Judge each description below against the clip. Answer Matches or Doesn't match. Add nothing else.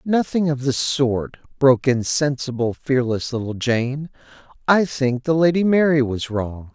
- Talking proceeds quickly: Doesn't match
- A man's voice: Matches